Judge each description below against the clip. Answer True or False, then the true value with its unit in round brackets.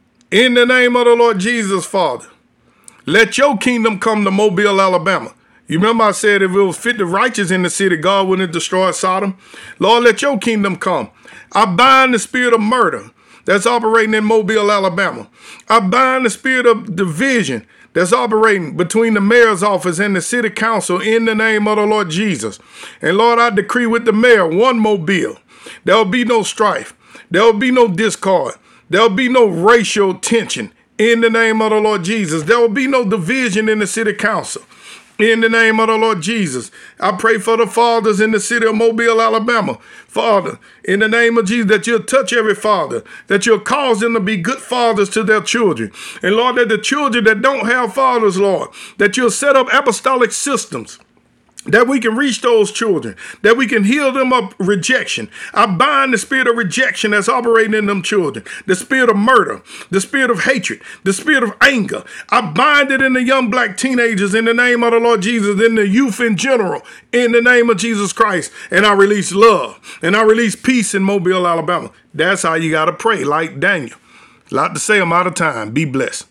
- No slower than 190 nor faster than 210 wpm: True (200 wpm)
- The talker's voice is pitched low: False (225 Hz)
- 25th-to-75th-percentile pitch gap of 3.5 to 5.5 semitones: False (2.8 semitones)